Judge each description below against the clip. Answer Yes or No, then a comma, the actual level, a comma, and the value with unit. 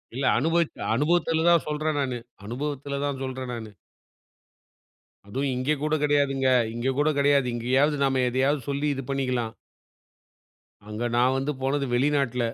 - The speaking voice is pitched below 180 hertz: Yes, medium, 140 Hz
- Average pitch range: No, narrow, 2.3 semitones